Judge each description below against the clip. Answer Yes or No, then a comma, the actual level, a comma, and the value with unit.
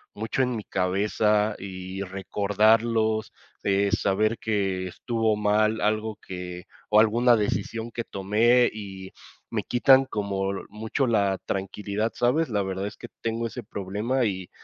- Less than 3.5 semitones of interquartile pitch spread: Yes, narrow, 2.4 semitones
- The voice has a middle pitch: No, low, 105 Hz